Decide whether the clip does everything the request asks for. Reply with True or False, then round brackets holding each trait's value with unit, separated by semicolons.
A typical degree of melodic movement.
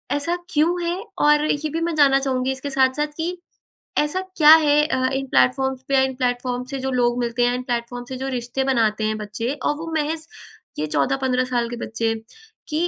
True (3.4 semitones)